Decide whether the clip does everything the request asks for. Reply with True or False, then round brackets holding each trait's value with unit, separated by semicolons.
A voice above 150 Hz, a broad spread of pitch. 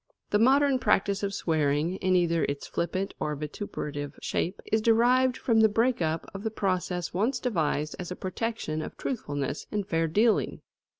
True (190 Hz; 5.7 semitones)